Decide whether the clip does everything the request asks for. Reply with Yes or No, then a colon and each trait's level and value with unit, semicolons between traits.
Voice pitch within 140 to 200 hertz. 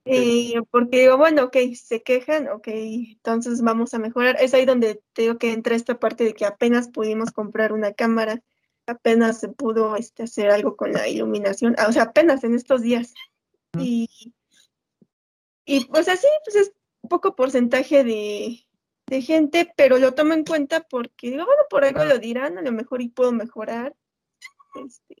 No: high, 245 Hz